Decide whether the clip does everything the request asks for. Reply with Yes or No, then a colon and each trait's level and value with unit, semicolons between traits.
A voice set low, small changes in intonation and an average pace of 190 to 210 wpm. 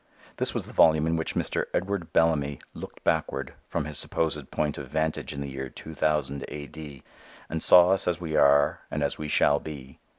Yes: very low, 75 Hz; narrow, 2.2 semitones; average, 200 wpm